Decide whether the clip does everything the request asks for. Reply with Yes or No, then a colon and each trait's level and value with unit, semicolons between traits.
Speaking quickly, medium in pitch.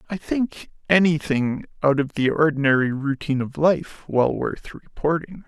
No: average, 145 wpm; medium, 150 Hz